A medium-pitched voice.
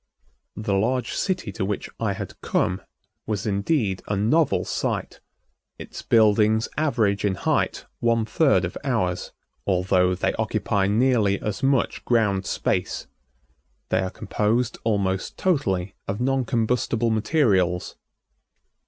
No: low, 105 Hz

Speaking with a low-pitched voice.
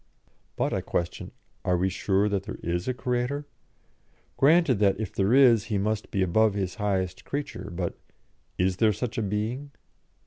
Yes: low, 105 Hz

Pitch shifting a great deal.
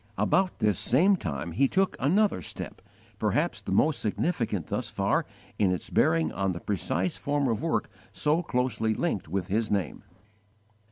Yes: wide, 8.5 semitones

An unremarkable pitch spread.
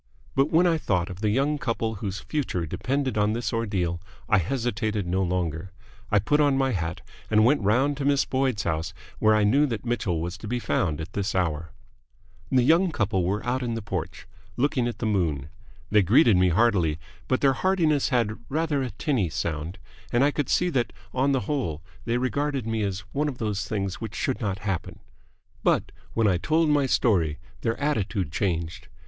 No: wide, 6.3 semitones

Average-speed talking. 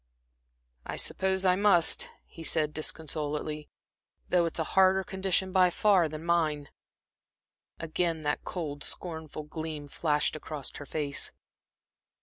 No: slow, 125 wpm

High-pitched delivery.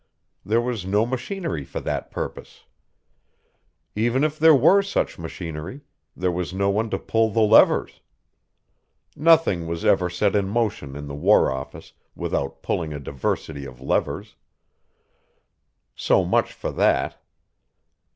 No: low, 100 Hz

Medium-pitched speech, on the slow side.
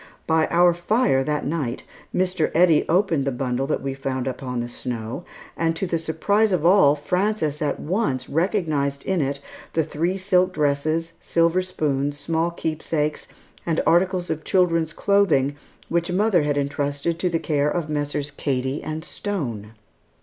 No: medium, 160 Hz; average, 160 wpm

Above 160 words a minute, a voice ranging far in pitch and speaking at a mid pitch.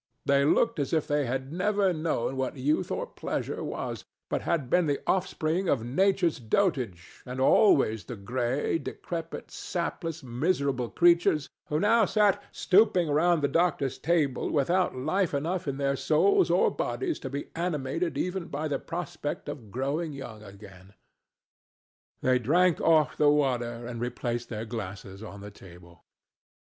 No: average, 155 wpm; wide, 5.8 semitones; medium, 145 Hz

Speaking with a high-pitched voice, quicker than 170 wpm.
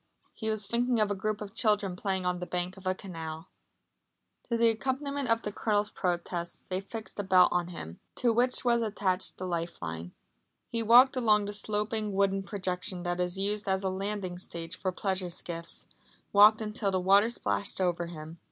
Yes: high, 195 Hz; average, 190 wpm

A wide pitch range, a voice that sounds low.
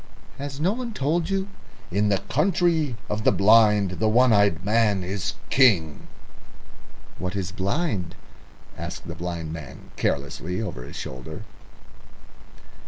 Yes: wide, 7.4 semitones; low, 105 Hz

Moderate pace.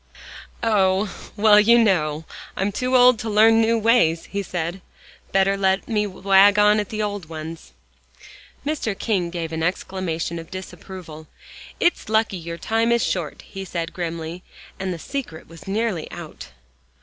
Yes: average, 155 wpm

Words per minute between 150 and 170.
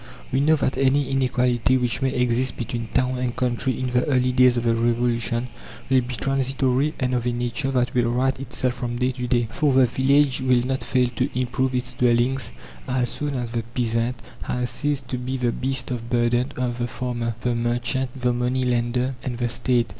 No: fast, 205 wpm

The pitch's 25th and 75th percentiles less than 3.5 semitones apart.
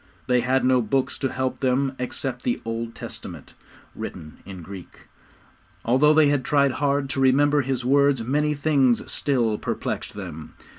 Yes: average, 2.8 semitones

